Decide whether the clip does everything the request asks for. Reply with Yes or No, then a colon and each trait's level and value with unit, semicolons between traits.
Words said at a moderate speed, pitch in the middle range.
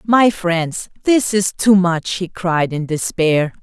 Yes: average, 165 wpm; medium, 180 Hz